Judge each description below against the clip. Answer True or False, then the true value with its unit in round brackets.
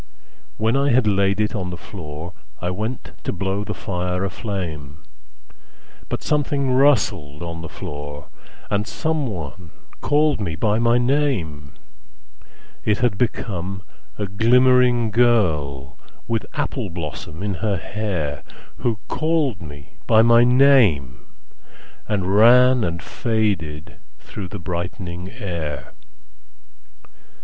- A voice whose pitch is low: True (100 Hz)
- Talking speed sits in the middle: False (105 wpm)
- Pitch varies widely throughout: True (6.2 semitones)